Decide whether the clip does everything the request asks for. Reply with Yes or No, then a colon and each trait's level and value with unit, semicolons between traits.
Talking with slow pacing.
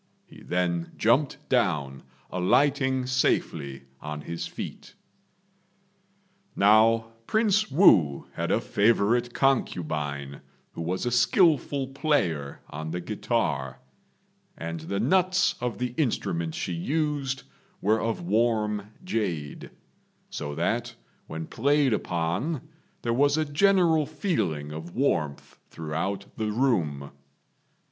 Yes: slow, 110 wpm